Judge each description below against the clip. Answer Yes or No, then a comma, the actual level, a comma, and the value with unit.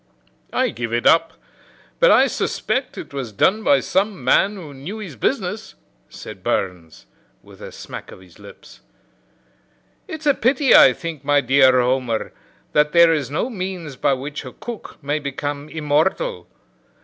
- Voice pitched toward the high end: No, medium, 150 Hz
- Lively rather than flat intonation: Yes, wide, 6.7 semitones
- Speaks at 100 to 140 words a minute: No, average, 160 wpm